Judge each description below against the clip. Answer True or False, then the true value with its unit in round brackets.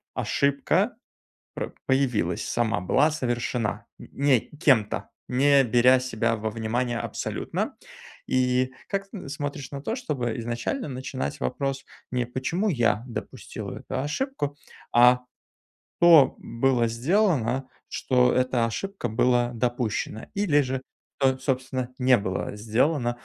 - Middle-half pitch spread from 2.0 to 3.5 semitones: True (2.9 semitones)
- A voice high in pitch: False (130 Hz)